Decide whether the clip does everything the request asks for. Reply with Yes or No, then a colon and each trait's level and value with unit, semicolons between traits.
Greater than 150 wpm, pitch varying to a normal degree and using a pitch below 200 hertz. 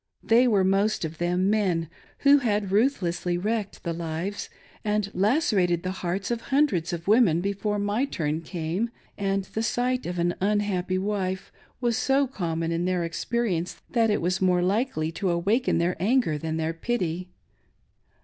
Yes: average, 165 wpm; average, 4.0 semitones; high, 190 Hz